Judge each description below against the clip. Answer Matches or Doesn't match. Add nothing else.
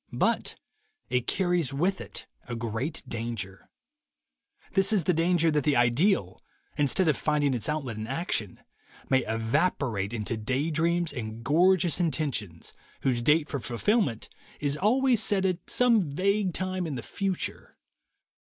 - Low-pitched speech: Doesn't match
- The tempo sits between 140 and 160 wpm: Matches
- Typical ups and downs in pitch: Doesn't match